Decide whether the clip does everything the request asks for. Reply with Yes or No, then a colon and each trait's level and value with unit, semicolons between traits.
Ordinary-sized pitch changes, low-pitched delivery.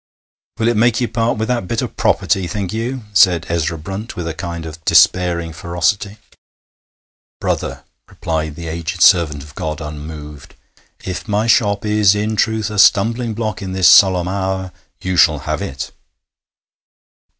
Yes: average, 4.5 semitones; very low, 95 Hz